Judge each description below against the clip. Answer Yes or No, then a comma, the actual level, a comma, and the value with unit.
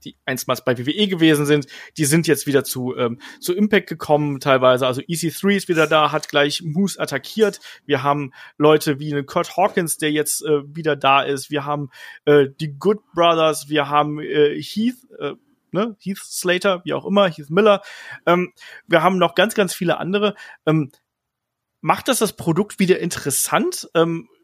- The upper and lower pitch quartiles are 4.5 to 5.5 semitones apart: Yes, average, 4.8 semitones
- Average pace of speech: Yes, average, 180 wpm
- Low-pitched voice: No, medium, 155 Hz